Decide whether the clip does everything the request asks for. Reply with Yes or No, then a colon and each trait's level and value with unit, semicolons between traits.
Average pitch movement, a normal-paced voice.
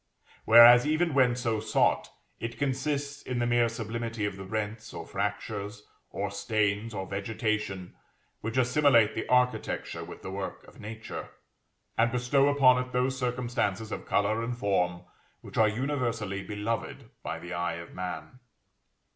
Yes: average, 3.5 semitones; average, 150 wpm